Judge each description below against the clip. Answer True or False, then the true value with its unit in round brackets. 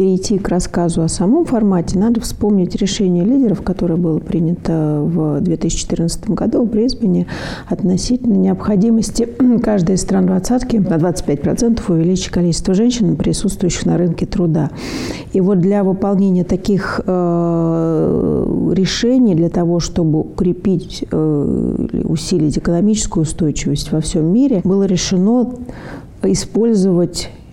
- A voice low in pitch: False (185 Hz)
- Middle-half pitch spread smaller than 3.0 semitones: False (3.6 semitones)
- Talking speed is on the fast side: False (115 wpm)